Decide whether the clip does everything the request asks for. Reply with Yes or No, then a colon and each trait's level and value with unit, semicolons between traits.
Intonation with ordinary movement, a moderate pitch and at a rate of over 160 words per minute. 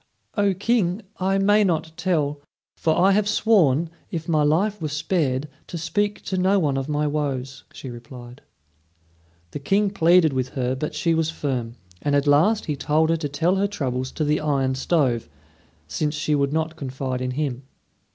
Yes: average, 4.9 semitones; medium, 155 Hz; average, 180 wpm